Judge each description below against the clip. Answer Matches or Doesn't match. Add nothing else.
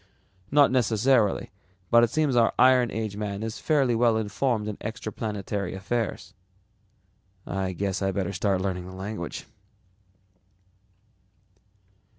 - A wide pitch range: Doesn't match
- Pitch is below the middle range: Matches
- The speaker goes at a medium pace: Doesn't match